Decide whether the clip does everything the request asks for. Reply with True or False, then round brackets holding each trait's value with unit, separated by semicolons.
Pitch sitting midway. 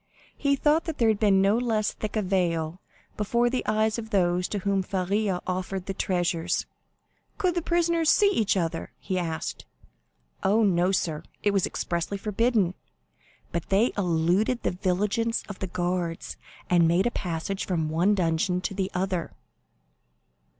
False (195 Hz)